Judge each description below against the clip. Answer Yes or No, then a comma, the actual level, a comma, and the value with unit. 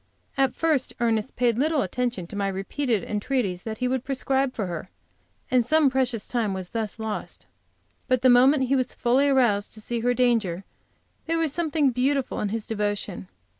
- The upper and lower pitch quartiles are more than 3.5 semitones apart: Yes, average, 4.1 semitones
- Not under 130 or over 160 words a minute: No, average, 180 wpm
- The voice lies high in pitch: Yes, high, 245 Hz